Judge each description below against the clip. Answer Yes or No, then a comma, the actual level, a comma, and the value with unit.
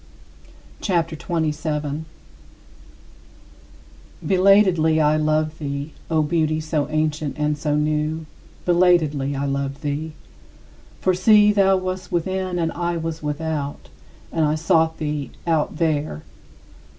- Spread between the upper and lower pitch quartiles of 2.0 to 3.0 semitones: Yes, narrow, 2.4 semitones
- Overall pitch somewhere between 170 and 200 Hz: No, medium, 155 Hz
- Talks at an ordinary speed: No, slow, 115 wpm